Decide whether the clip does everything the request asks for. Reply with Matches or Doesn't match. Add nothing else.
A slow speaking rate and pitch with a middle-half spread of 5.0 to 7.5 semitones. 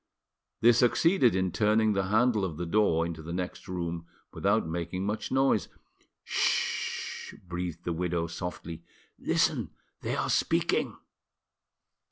Doesn't match